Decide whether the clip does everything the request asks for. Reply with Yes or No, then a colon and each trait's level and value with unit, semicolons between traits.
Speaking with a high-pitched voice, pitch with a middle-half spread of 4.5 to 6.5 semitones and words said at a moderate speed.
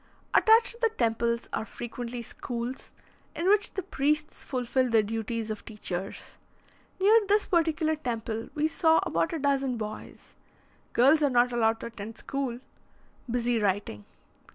Yes: high, 245 Hz; wide, 5.4 semitones; average, 145 wpm